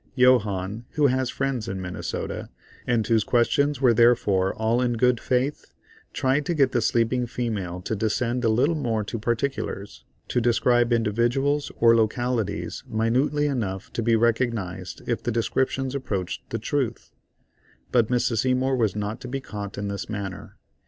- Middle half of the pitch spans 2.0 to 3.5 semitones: Yes, average, 2.9 semitones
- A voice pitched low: Yes, low, 120 Hz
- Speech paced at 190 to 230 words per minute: No, average, 160 wpm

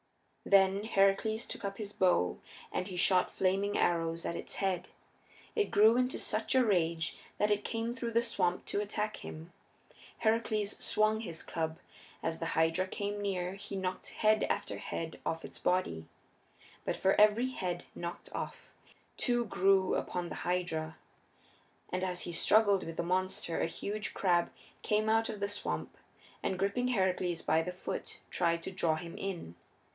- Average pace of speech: Yes, average, 165 wpm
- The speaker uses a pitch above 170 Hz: Yes, high, 190 Hz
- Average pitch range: Yes, average, 3.4 semitones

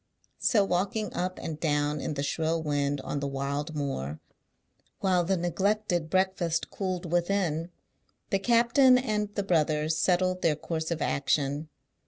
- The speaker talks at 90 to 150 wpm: Yes, average, 145 wpm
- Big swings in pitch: No, average, 4.3 semitones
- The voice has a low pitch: No, medium, 170 Hz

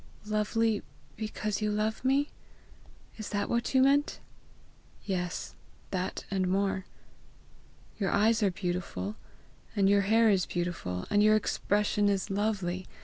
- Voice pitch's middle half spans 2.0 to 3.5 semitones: Yes, narrow, 2.5 semitones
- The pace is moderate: No, slow, 130 wpm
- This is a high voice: Yes, high, 205 Hz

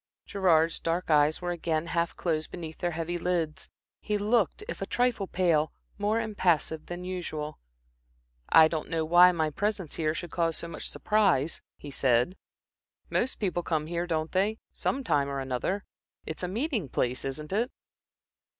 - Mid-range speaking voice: Yes, medium, 170 Hz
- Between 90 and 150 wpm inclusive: No, average, 170 wpm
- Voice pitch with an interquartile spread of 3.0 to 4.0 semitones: Yes, average, 3.4 semitones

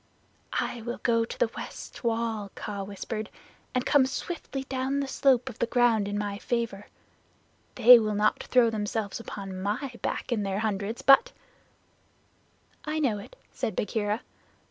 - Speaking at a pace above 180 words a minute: No, average, 165 wpm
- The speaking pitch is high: Yes, high, 225 Hz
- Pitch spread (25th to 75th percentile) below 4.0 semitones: Yes, average, 3.4 semitones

